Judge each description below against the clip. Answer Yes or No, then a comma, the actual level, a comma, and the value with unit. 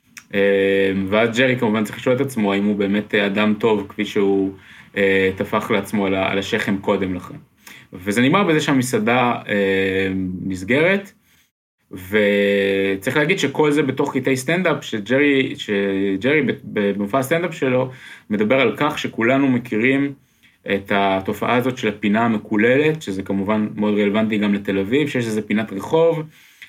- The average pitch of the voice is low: Yes, low, 105 Hz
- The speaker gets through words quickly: No, average, 135 wpm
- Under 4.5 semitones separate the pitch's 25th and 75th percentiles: No, average, 5.1 semitones